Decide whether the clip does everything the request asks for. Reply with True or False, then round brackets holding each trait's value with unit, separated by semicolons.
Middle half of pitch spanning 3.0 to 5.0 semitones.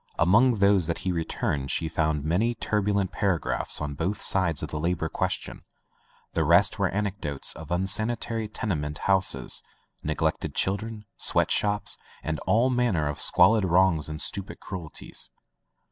True (4.6 semitones)